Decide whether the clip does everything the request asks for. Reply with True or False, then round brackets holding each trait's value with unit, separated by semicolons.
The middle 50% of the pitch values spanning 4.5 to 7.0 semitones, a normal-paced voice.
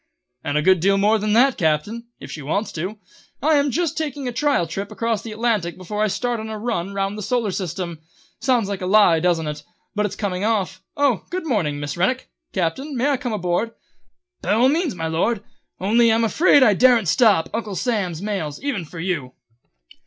False (5.1 semitones; 210 wpm)